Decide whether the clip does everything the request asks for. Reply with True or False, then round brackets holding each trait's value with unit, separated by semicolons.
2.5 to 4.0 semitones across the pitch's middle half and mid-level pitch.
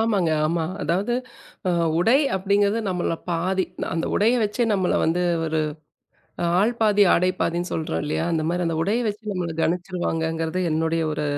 True (3.7 semitones; 180 Hz)